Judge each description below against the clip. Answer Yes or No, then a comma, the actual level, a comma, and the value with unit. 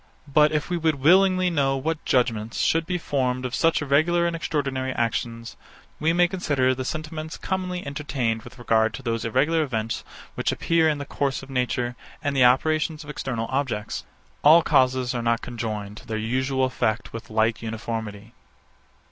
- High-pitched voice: No, low, 135 Hz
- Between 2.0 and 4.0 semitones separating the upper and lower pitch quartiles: No, average, 5.1 semitones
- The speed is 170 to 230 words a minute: Yes, average, 175 wpm